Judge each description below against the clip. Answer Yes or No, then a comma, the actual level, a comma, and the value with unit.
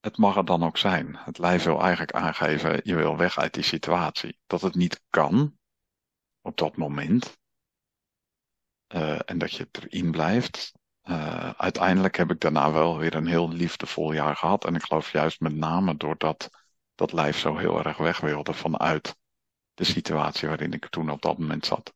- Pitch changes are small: Yes, narrow, 2.1 semitones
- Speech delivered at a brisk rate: No, average, 180 wpm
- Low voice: Yes, very low, 80 Hz